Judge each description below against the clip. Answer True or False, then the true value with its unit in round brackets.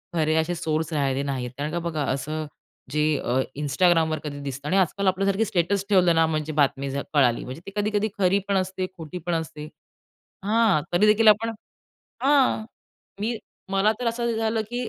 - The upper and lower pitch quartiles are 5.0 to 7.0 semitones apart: True (5.3 semitones)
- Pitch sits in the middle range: True (170 Hz)